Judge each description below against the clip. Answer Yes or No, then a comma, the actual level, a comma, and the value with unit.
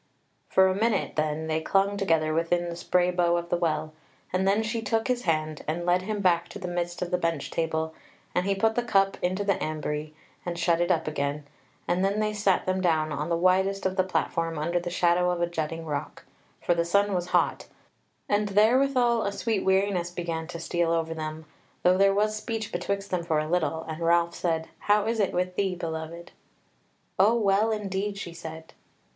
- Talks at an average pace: No, fast, 210 wpm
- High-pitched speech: No, medium, 175 Hz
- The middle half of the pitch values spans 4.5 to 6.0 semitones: No, average, 3.3 semitones